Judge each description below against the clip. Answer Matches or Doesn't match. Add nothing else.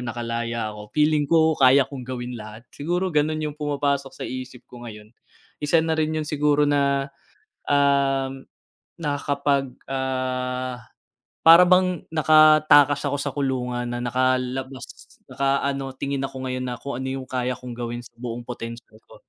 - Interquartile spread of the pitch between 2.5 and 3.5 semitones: Matches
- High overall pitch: Doesn't match